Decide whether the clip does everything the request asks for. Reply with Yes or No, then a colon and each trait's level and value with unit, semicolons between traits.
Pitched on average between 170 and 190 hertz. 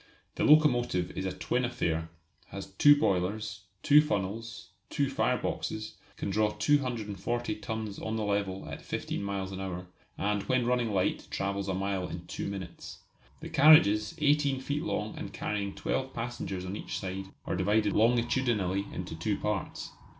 No: low, 105 Hz